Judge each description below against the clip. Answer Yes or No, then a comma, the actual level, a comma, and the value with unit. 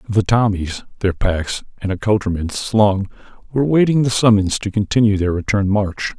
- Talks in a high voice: No, low, 105 Hz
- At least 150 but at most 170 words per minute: Yes, average, 155 wpm